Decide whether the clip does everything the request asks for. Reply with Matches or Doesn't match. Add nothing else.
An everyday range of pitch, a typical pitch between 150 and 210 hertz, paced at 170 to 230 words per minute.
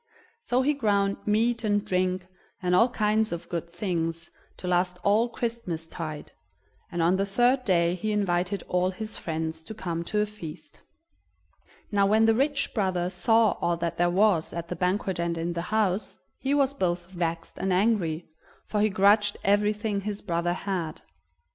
Matches